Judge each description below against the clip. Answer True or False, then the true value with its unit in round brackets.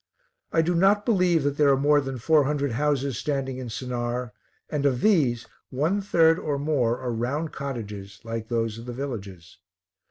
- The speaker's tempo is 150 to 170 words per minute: False (180 wpm)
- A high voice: False (135 Hz)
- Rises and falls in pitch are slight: False (4.0 semitones)